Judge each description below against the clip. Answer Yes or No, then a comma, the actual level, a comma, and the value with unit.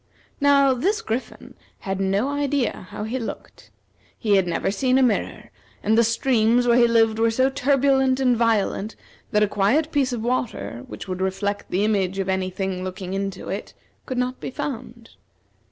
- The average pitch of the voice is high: Yes, high, 225 Hz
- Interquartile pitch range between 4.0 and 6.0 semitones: Yes, average, 4.9 semitones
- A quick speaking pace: No, average, 180 wpm